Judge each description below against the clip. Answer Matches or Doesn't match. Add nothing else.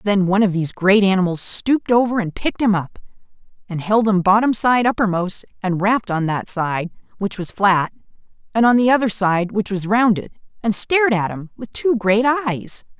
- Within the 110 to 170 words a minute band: Doesn't match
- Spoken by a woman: Matches